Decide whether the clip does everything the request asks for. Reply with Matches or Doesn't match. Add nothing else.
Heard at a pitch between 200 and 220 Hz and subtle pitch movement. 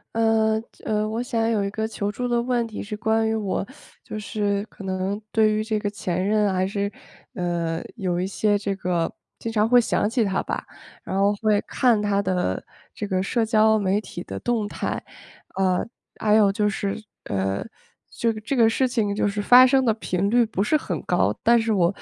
Matches